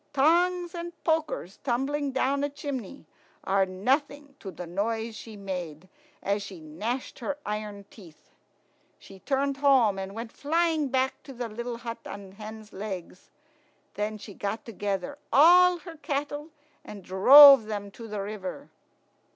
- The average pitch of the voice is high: Yes, high, 230 Hz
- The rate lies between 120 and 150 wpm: Yes, average, 145 wpm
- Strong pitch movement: Yes, wide, 6.2 semitones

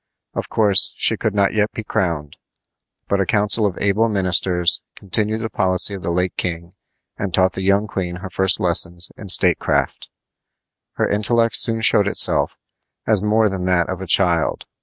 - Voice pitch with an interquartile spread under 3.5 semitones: Yes, average, 2.7 semitones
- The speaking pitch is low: Yes, very low, 95 Hz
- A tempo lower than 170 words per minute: No, average, 175 wpm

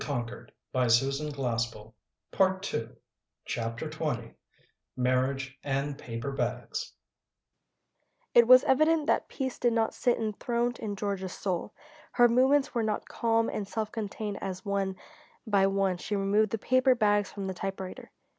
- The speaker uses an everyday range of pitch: No, wide, 6.6 semitones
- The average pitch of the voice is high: Yes, high, 200 Hz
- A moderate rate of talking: No, slow, 130 wpm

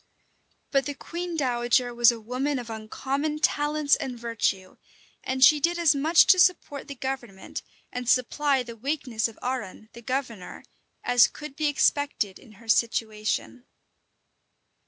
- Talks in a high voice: Yes, very high, 255 Hz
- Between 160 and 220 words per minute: No, average, 145 wpm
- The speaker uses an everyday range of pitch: Yes, average, 3.8 semitones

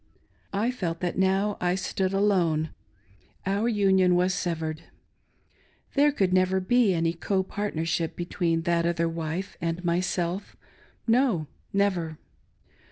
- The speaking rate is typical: No, slow, 125 wpm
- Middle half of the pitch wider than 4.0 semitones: No, average, 2.9 semitones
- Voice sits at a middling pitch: Yes, medium, 180 Hz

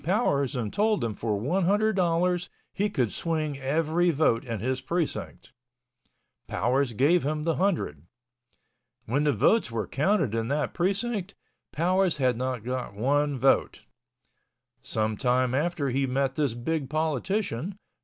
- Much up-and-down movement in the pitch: Yes, wide, 5.7 semitones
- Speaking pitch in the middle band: Yes, medium, 145 Hz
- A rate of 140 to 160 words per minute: Yes, average, 145 wpm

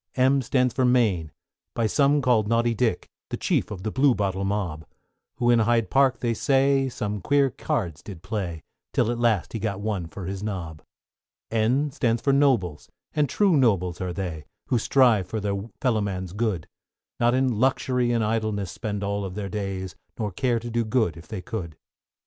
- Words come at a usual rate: Yes, average, 185 wpm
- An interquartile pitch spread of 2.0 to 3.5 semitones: No, average, 4.4 semitones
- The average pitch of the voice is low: Yes, low, 110 Hz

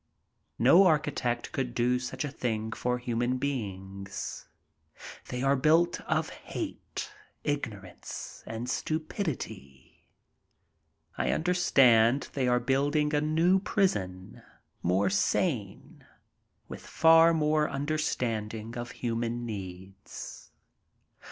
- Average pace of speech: No, slow, 100 wpm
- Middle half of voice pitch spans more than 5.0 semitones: Yes, wide, 5.5 semitones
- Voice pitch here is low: Yes, low, 125 Hz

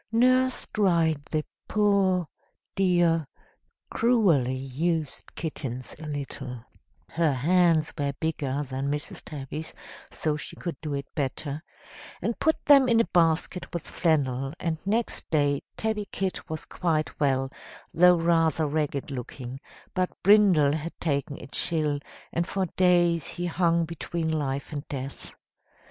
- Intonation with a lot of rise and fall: No, average, 4.0 semitones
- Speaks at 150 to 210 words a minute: No, slow, 135 wpm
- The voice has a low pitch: No, medium, 160 Hz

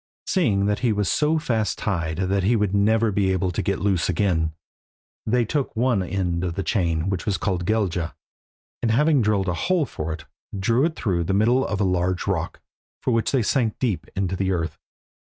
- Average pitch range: Yes, average, 4.0 semitones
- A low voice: Yes, low, 100 Hz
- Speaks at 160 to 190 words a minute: No, fast, 205 wpm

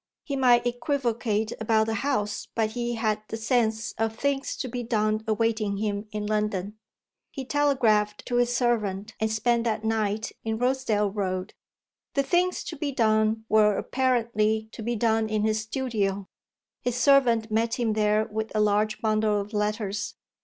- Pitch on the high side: Yes, high, 220 Hz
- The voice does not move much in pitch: Yes, narrow, 2.2 semitones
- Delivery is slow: No, average, 165 wpm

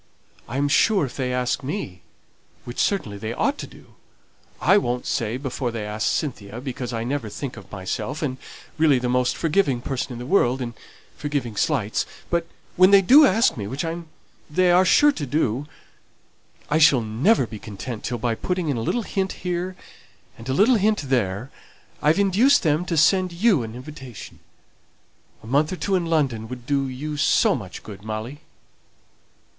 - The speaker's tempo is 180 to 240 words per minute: Yes, average, 185 wpm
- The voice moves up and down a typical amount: No, wide, 6.6 semitones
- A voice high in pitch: No, low, 135 Hz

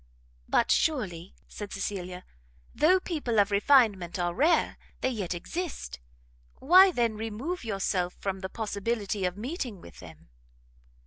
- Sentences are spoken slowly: Yes, slow, 130 wpm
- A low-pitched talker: No, high, 210 Hz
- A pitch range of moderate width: No, wide, 6.0 semitones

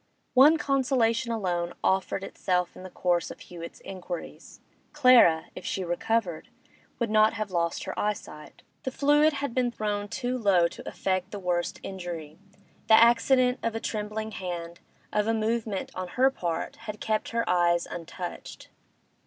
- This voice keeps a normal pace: Yes, average, 155 wpm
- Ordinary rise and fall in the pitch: Yes, average, 4.8 semitones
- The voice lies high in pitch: Yes, high, 210 Hz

